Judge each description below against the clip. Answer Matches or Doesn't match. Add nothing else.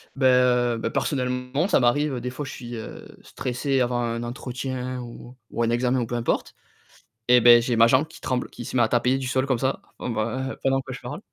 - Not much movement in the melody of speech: Matches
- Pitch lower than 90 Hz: Doesn't match